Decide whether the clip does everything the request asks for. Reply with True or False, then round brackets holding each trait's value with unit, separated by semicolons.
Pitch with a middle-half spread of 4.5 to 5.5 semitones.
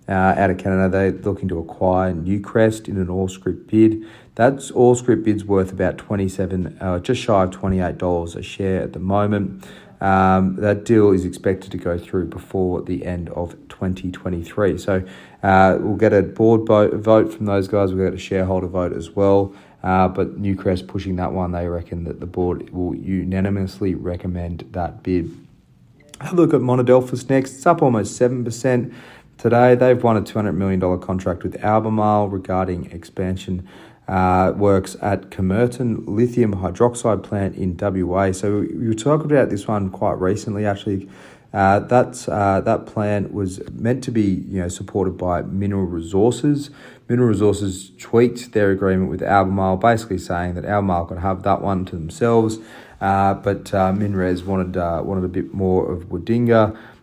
False (2.8 semitones)